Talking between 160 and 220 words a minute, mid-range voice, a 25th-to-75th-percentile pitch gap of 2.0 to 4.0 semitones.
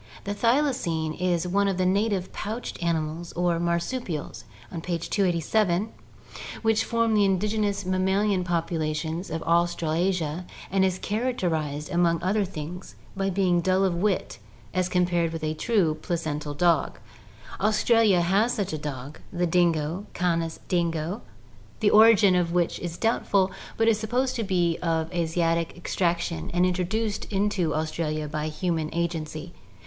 No: average, 145 wpm; medium, 175 Hz; average, 3.3 semitones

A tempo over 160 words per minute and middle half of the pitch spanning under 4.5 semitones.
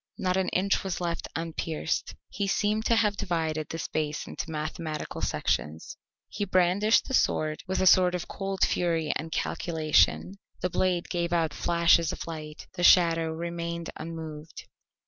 No: average, 155 wpm; narrow, 2.5 semitones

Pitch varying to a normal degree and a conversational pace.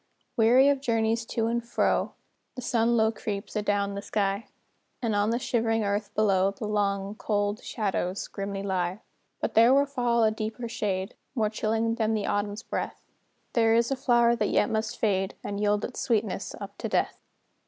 No: narrow, 2.3 semitones; average, 180 wpm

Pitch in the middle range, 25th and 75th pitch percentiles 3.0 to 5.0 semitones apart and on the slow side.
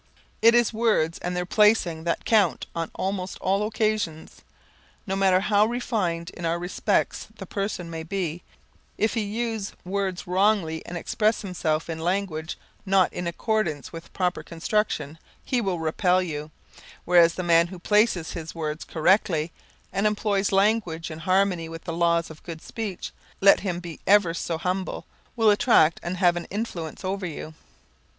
No: medium, 180 Hz; average, 3.7 semitones; average, 165 wpm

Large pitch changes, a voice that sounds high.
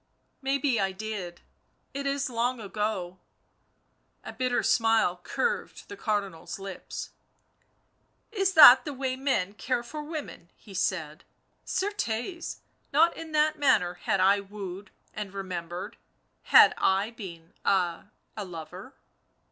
Yes: wide, 6.7 semitones; high, 215 Hz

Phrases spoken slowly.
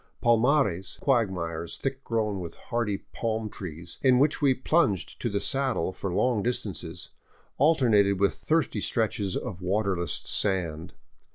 Yes: slow, 130 wpm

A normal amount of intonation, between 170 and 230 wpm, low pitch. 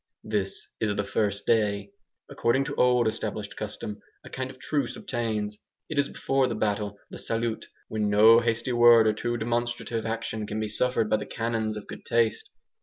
No: narrow, 2.1 semitones; average, 180 wpm; low, 110 Hz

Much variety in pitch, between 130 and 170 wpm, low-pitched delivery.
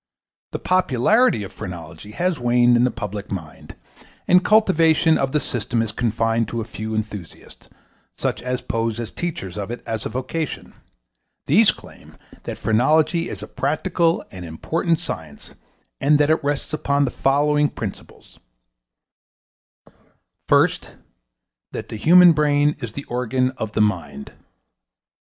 Yes: wide, 5.9 semitones; average, 140 wpm; low, 125 Hz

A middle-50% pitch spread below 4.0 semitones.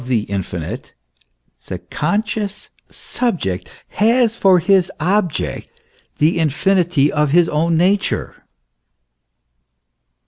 No: average, 5.1 semitones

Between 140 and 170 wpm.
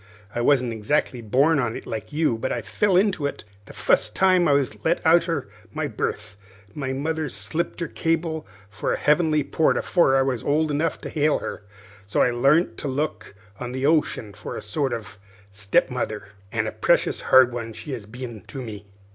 No: average, 200 wpm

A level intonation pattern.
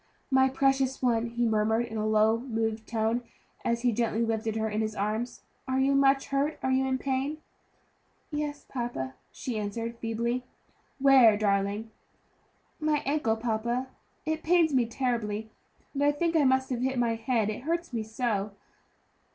No: average, 3.3 semitones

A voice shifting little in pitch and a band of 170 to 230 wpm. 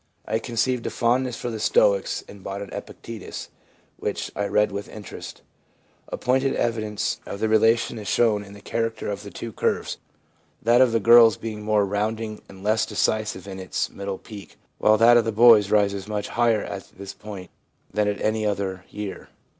Yes: narrow, 2.2 semitones; average, 185 wpm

